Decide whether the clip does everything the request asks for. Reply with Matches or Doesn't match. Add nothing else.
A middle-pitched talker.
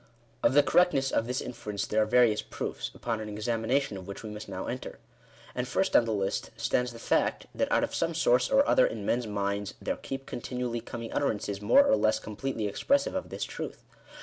Doesn't match